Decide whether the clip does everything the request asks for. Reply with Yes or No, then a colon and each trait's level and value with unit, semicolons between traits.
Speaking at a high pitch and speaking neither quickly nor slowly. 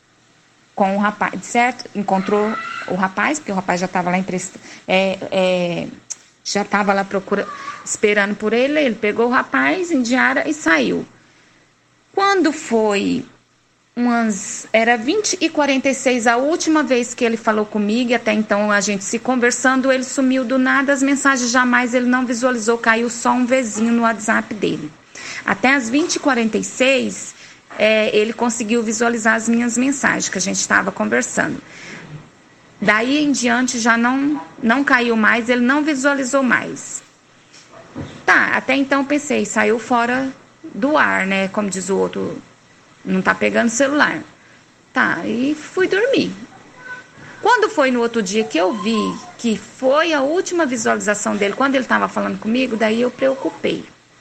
Yes: high, 240 Hz; average, 155 wpm